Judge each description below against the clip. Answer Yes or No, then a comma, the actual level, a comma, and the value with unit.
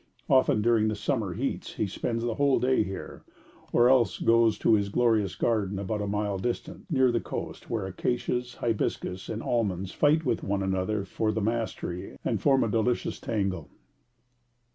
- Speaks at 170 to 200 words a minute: Yes, average, 175 wpm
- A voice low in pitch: Yes, low, 110 Hz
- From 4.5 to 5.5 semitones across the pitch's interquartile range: No, average, 3.3 semitones